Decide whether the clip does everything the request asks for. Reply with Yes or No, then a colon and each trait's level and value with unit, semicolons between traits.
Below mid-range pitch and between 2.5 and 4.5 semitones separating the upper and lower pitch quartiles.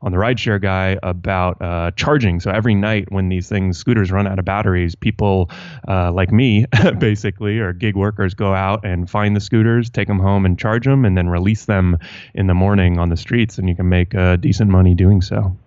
Yes: low, 100 Hz; average, 2.8 semitones